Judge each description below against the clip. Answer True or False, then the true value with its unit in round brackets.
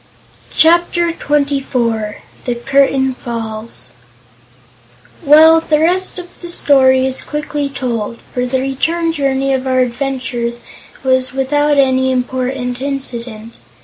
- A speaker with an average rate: False (115 wpm)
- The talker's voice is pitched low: False (265 Hz)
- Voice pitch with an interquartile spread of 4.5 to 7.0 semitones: False (2.8 semitones)